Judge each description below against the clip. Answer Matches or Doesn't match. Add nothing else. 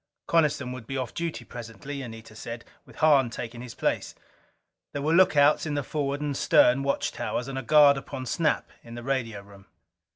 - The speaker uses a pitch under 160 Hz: Matches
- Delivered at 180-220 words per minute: Matches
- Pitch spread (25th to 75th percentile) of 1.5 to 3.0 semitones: Doesn't match